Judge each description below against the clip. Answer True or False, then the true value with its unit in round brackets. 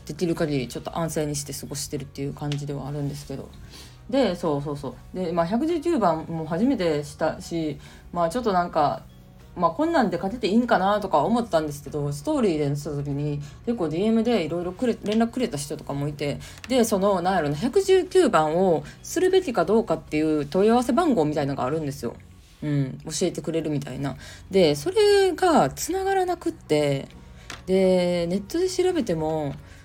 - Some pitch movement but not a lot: False (8.1 semitones)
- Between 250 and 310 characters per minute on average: False (380 characters per minute)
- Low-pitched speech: False (165 Hz)